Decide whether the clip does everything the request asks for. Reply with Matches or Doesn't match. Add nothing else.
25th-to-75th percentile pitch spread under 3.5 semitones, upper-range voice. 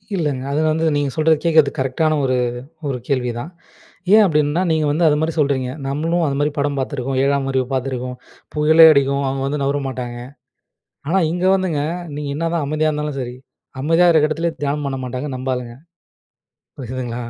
Doesn't match